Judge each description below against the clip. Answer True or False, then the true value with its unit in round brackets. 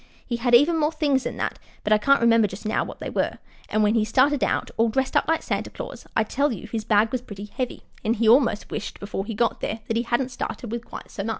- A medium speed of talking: False (270 wpm)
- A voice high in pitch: True (230 Hz)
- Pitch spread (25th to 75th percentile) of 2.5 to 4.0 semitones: True (3.2 semitones)